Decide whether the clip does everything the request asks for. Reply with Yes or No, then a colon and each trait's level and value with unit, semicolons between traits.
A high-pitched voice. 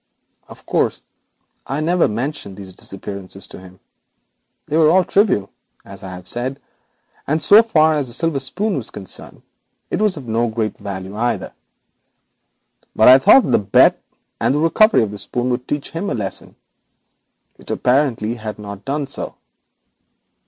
No: low, 125 Hz